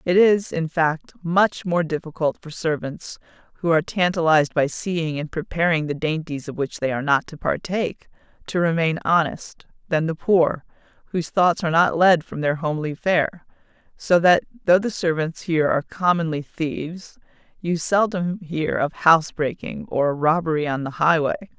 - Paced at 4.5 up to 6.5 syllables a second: Yes, 4.9 syllables/s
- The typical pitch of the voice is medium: Yes, medium, 165 Hz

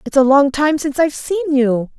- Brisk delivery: Yes, fast, 240 wpm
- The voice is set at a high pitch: Yes, very high, 275 Hz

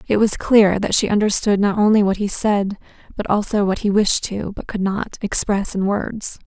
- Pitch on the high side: Yes, high, 205 Hz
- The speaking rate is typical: No, fast, 210 wpm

